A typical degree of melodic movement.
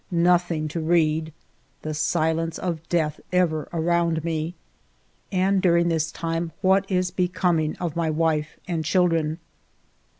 No: narrow, 1.9 semitones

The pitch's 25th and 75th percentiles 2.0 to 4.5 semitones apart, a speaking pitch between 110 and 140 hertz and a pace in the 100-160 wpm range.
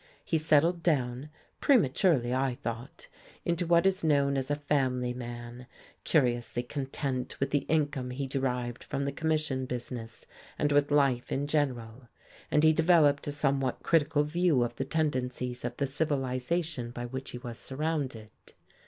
Yes: average, 3.3 semitones; low, 135 Hz; average, 155 wpm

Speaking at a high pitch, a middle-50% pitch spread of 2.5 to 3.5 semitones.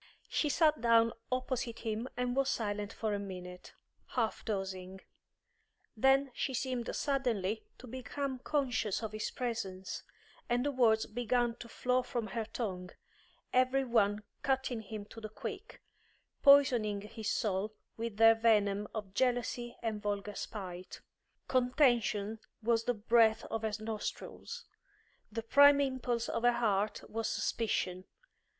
Yes: high, 230 Hz; average, 3.2 semitones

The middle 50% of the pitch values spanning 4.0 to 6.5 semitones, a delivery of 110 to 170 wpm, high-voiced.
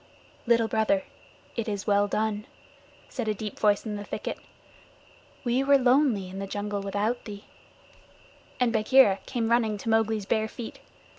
No: narrow, 2.5 semitones; average, 155 wpm; high, 220 Hz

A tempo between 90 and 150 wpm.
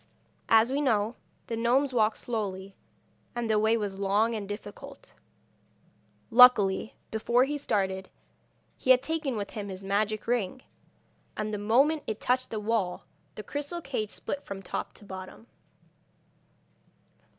Yes: average, 140 wpm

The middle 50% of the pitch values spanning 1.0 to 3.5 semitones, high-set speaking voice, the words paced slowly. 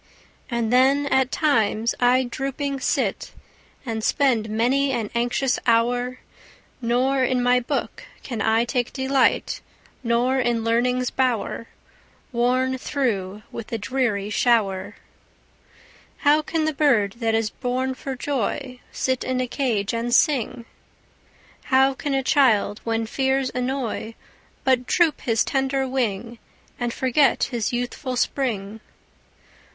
Yes: narrow, 2.6 semitones; very high, 250 Hz; slow, 130 wpm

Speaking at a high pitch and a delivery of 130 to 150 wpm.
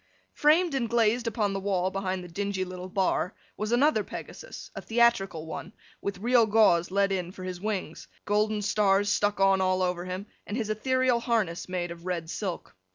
No: high, 200 Hz; average, 175 wpm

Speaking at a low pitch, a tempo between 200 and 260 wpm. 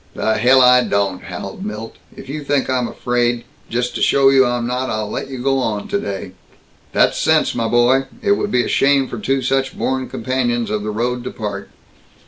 Yes: low, 125 Hz; fast, 205 wpm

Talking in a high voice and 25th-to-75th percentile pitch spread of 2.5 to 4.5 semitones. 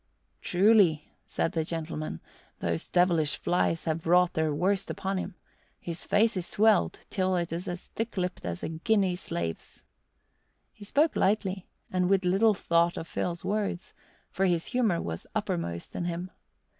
No: medium, 180 Hz; average, 3.1 semitones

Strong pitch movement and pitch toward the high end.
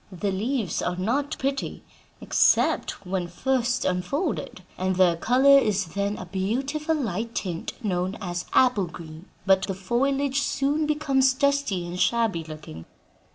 Yes: wide, 6.9 semitones; high, 210 Hz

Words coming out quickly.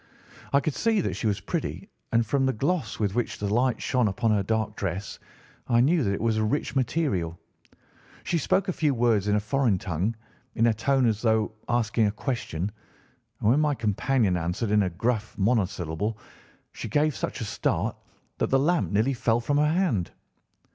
No: average, 195 wpm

